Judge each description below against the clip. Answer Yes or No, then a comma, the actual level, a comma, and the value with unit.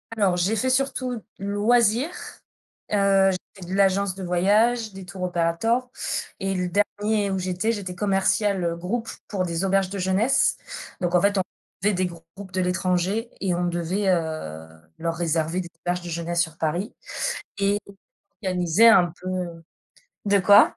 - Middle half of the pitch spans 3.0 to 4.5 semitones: No, narrow, 2.6 semitones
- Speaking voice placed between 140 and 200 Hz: Yes, high, 190 Hz